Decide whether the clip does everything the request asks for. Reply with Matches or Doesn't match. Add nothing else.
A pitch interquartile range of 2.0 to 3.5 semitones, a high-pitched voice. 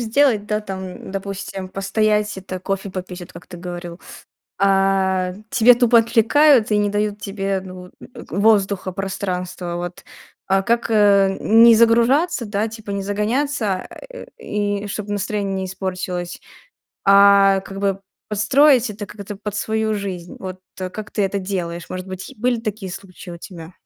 Matches